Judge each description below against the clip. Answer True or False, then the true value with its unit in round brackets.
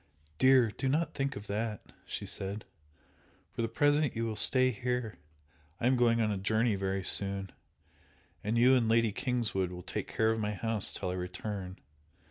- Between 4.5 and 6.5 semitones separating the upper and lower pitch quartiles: False (3.8 semitones)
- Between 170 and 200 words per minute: True (180 wpm)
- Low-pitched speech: True (110 Hz)